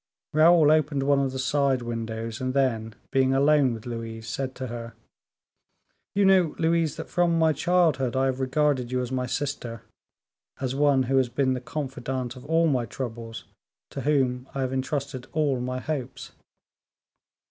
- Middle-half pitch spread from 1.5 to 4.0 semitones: Yes, average, 2.9 semitones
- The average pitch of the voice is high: No, low, 130 Hz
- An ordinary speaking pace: Yes, average, 170 wpm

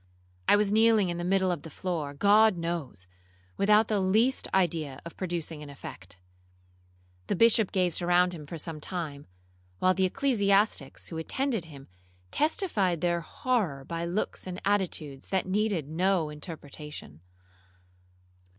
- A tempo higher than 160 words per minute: No, average, 140 wpm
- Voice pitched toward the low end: No, medium, 180 Hz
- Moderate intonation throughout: Yes, average, 4.5 semitones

